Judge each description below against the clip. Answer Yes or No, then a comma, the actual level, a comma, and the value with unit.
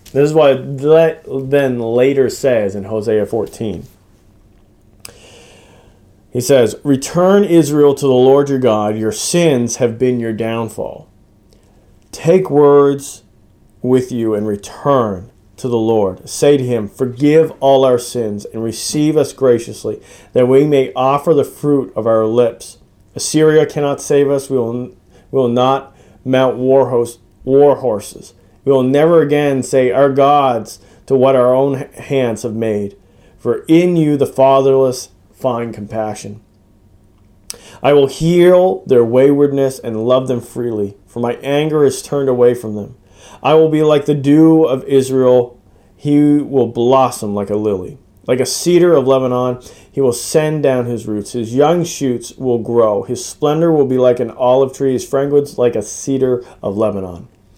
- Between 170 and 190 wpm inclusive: No, average, 155 wpm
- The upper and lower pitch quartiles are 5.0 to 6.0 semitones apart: No, average, 4.4 semitones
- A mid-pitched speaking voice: No, low, 125 Hz